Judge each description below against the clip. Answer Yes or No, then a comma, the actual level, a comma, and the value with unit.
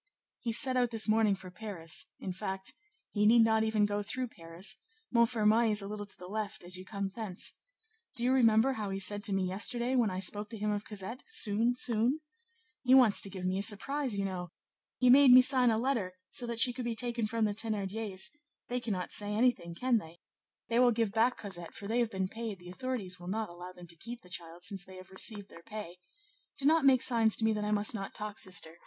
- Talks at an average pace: No, fast, 235 wpm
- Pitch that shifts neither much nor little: Yes, average, 3.6 semitones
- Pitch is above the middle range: Yes, high, 215 Hz